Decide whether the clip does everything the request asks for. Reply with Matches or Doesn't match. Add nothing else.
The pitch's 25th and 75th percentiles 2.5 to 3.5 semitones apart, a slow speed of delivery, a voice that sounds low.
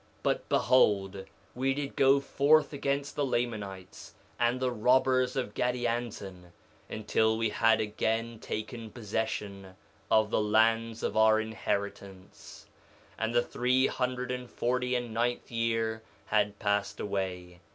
Matches